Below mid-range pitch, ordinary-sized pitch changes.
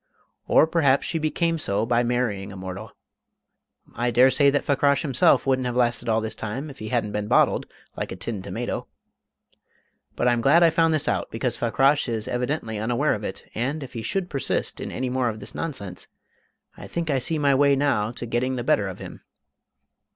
Yes: low, 125 Hz; average, 4.4 semitones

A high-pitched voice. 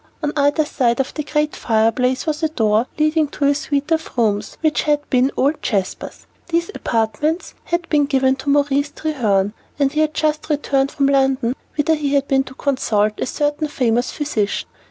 Yes: very high, 280 Hz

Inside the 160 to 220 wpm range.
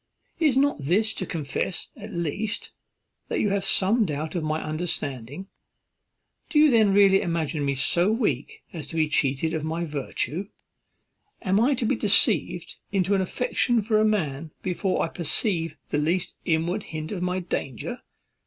Yes: average, 165 wpm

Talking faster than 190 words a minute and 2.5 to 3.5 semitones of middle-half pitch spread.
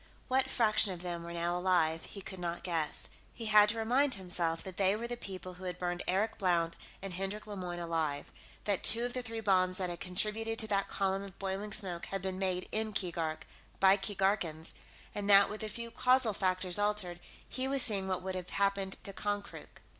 Yes: fast, 205 wpm; average, 2.9 semitones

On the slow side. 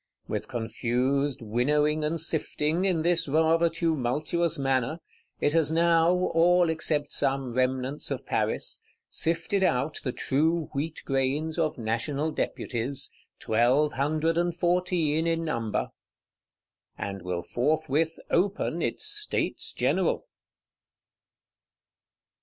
Yes: slow, 110 wpm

